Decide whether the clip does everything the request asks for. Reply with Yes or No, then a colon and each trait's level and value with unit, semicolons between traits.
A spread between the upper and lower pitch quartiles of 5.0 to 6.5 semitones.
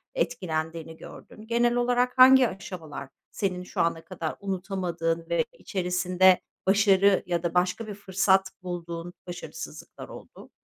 No: average, 2.8 semitones